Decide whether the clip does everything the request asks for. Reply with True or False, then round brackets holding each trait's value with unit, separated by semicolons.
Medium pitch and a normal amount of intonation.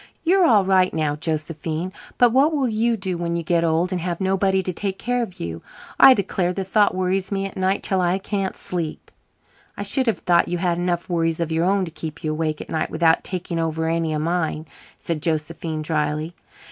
True (175 Hz; 3.0 semitones)